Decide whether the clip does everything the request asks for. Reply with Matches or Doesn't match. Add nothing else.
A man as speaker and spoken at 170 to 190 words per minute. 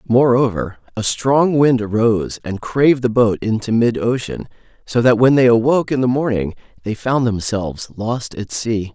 Matches